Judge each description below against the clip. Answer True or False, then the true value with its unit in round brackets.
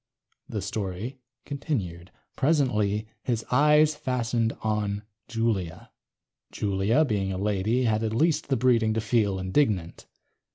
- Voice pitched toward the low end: True (110 Hz)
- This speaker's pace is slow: True (120 wpm)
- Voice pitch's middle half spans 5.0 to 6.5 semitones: False (4.2 semitones)